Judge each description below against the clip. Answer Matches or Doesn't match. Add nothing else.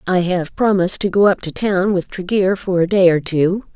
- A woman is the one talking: Matches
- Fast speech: Matches